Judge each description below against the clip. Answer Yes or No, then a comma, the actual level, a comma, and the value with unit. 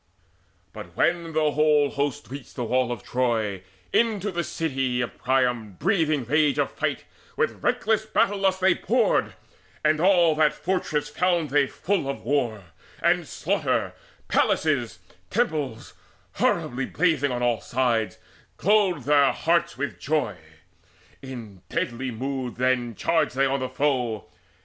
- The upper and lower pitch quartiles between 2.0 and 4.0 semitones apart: No, average, 4.8 semitones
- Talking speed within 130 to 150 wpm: Yes, average, 140 wpm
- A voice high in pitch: No, medium, 140 Hz